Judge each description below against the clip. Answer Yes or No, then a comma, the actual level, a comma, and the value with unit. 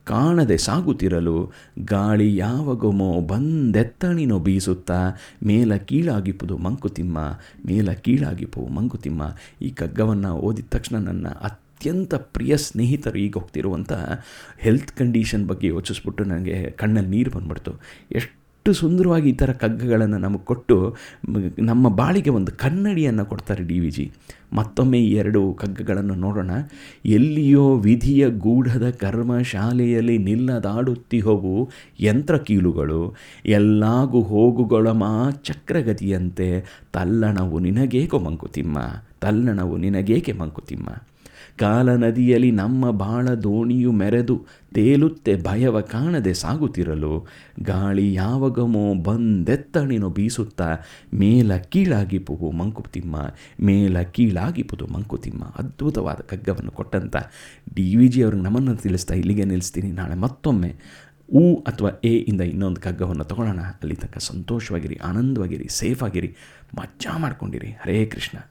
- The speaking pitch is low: Yes, low, 105 Hz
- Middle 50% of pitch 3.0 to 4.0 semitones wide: No, average, 4.7 semitones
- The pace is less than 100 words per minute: No, fast, 105 wpm